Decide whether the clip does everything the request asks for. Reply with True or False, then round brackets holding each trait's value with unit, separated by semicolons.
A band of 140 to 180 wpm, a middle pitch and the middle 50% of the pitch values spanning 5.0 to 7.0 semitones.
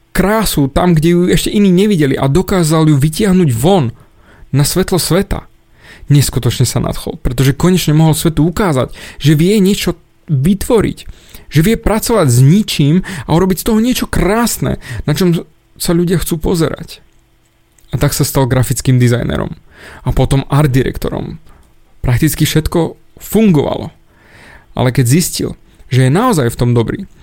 True (145 wpm; 155 Hz; 5.5 semitones)